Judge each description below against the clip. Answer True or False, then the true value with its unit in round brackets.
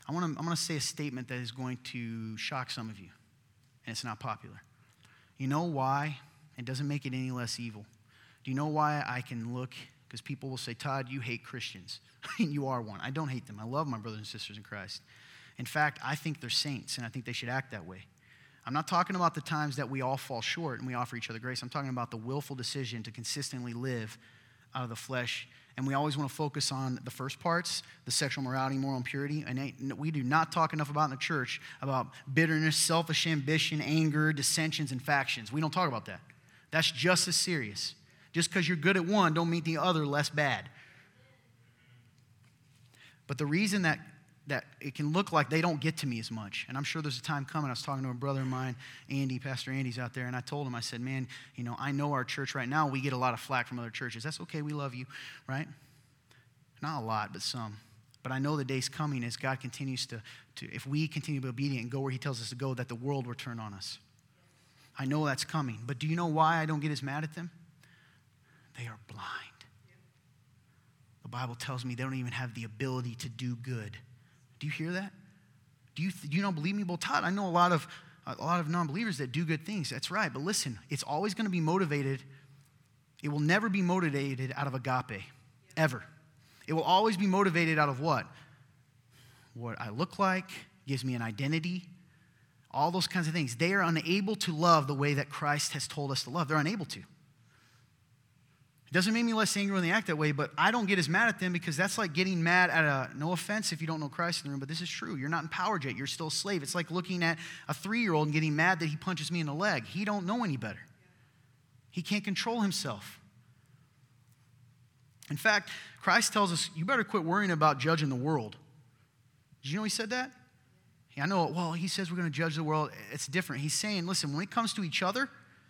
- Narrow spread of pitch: False (4.2 semitones)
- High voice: False (140 Hz)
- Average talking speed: False (235 wpm)